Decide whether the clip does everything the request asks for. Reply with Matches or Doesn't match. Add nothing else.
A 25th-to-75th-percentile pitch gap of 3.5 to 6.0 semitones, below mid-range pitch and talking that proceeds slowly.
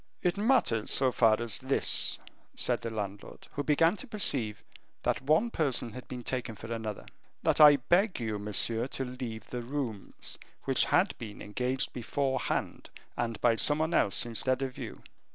Doesn't match